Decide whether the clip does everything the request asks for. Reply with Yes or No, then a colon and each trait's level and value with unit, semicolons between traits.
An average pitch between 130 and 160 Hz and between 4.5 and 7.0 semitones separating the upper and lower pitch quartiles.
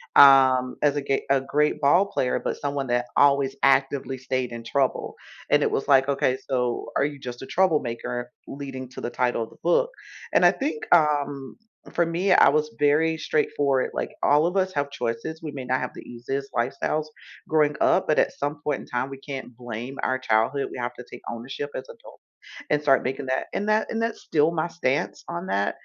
No: medium, 140 Hz; average, 2.9 semitones